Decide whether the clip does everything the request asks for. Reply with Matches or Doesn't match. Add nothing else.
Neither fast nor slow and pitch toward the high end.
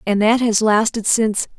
Matches